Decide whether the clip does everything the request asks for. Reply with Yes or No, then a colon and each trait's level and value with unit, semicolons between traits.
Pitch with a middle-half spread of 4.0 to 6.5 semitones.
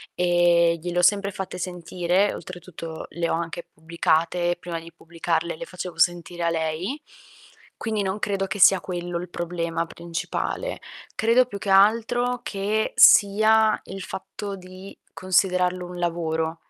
No: average, 2.7 semitones